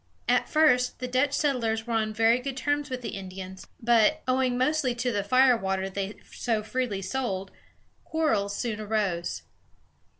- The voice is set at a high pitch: Yes, high, 235 Hz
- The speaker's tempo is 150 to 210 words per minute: Yes, average, 160 wpm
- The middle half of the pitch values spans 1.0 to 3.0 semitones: No, average, 4.2 semitones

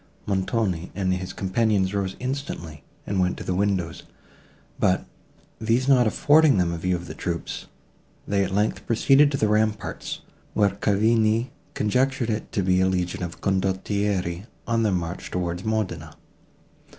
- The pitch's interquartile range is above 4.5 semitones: No, average, 3.4 semitones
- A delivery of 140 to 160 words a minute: Yes, average, 150 wpm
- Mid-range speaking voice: No, low, 100 Hz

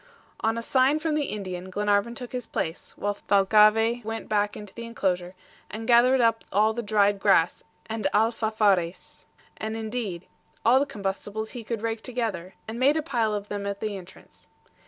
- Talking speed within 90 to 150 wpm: No, average, 175 wpm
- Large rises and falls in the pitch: No, narrow, 2.6 semitones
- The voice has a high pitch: Yes, high, 215 Hz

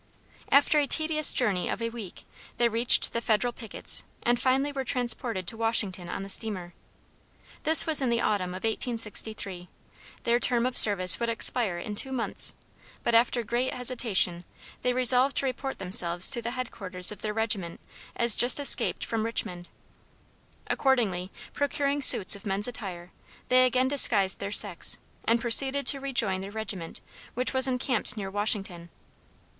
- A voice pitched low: No, high, 230 Hz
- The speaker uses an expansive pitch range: No, average, 4.5 semitones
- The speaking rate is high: No, average, 160 wpm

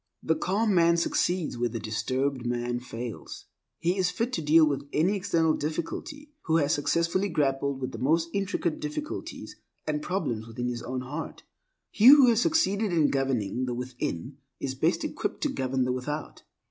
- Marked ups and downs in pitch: Yes, wide, 5.8 semitones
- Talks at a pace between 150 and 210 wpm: Yes, average, 170 wpm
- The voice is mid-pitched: Yes, medium, 150 Hz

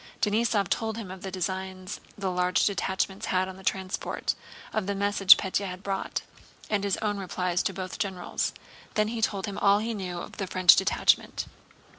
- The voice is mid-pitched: No, high, 195 Hz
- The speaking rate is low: No, average, 185 wpm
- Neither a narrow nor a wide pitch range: No, narrow, 1.6 semitones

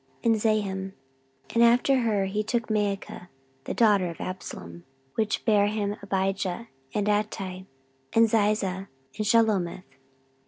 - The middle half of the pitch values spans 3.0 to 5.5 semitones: No, narrow, 2.4 semitones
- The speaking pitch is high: Yes, high, 205 Hz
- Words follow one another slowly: Yes, slow, 120 wpm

